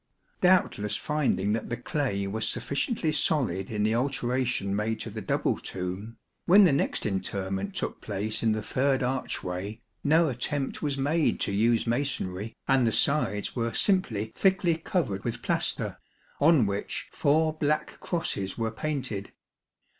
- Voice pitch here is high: No, low, 120 Hz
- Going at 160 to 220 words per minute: No, average, 145 wpm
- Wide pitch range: Yes, wide, 6.2 semitones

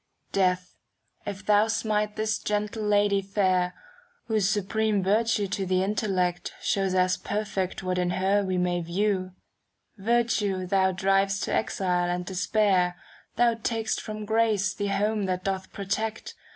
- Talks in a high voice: Yes, high, 195 Hz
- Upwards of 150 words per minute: No, average, 145 wpm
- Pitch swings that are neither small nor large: No, narrow, 2.3 semitones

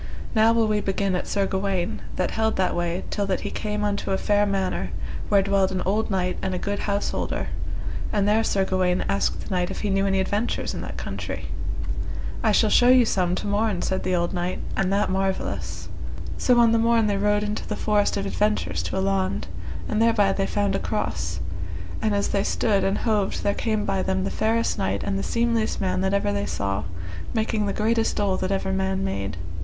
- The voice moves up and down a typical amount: No, narrow, 2.2 semitones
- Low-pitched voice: No, high, 195 Hz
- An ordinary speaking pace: No, fast, 215 wpm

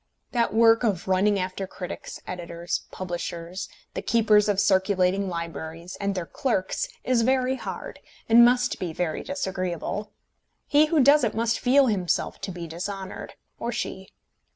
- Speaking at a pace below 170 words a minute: Yes, average, 150 wpm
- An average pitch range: Yes, average, 4.4 semitones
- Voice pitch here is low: No, high, 195 Hz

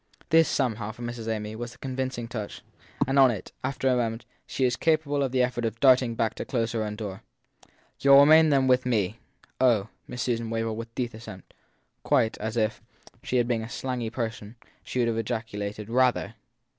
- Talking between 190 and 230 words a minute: Yes, average, 200 wpm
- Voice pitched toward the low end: Yes, low, 120 Hz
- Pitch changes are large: No, narrow, 2.5 semitones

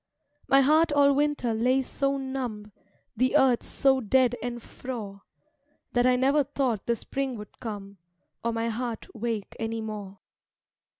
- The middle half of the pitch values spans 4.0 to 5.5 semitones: No, average, 3.2 semitones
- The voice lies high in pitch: Yes, high, 245 Hz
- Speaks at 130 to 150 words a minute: Yes, average, 145 wpm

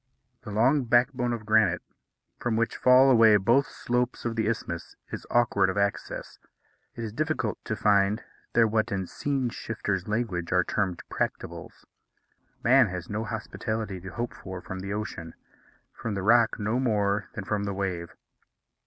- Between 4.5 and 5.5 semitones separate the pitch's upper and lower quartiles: No, average, 3.3 semitones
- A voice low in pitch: Yes, low, 110 Hz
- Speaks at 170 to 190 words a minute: No, average, 160 wpm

